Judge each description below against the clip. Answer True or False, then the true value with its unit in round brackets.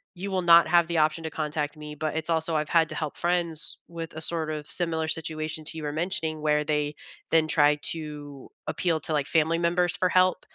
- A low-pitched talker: False (160 Hz)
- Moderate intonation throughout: False (1.8 semitones)